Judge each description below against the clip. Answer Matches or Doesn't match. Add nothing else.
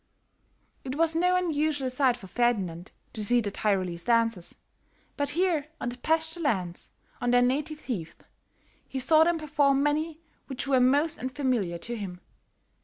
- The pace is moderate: Matches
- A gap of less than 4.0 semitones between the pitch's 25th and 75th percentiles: Doesn't match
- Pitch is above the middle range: Matches